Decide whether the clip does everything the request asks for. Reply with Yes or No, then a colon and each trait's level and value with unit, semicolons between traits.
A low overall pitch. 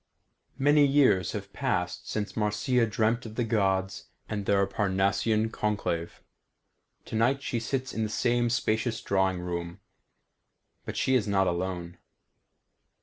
Yes: low, 105 Hz